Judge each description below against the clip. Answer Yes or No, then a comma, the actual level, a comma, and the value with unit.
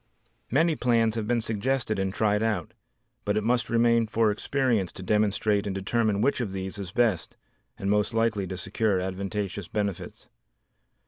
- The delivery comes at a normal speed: Yes, average, 165 wpm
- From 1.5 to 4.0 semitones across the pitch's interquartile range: Yes, average, 2.8 semitones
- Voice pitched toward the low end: Yes, low, 105 Hz